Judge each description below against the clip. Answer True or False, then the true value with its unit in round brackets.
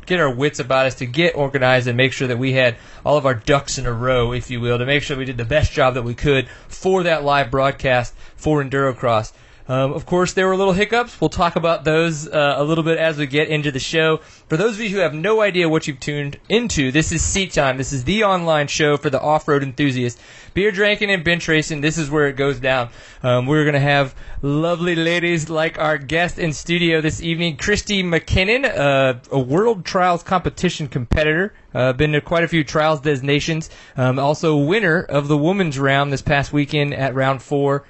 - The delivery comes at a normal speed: False (225 wpm)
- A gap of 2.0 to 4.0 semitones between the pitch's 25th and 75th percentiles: True (3.5 semitones)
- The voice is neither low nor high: True (150 Hz)